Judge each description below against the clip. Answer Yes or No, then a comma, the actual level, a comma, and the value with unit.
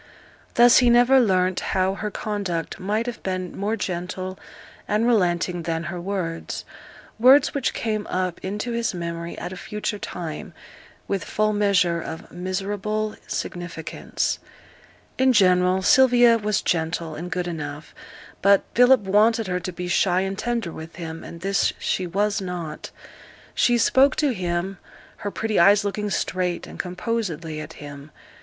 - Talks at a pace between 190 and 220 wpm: No, average, 150 wpm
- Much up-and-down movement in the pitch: No, average, 3.5 semitones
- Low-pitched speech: No, high, 190 Hz